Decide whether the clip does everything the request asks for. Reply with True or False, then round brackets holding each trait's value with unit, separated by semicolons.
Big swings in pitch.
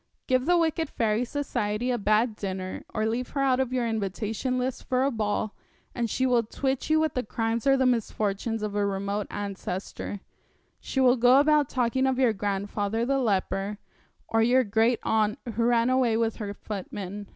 False (3.6 semitones)